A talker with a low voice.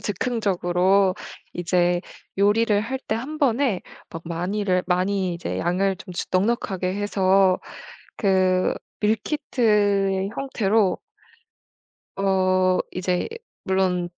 No: high, 190 Hz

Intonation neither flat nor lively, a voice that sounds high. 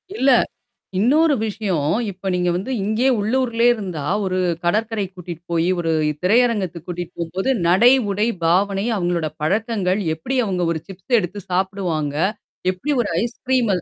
Yes: average, 4.1 semitones; high, 195 Hz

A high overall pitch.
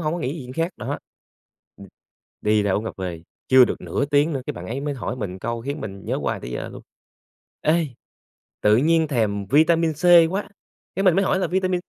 No: medium, 140 Hz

